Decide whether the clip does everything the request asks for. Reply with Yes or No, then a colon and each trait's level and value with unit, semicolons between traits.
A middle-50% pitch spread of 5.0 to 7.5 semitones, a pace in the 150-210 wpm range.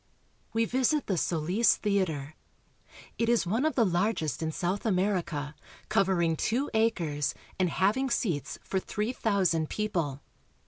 No: wide, 5.5 semitones; slow, 135 wpm